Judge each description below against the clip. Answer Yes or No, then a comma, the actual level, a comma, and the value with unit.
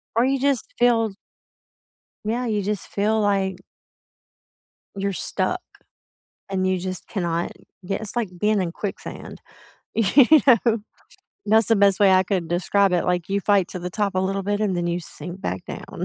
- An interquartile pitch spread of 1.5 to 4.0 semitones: Yes, average, 2.9 semitones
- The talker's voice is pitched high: Yes, high, 200 Hz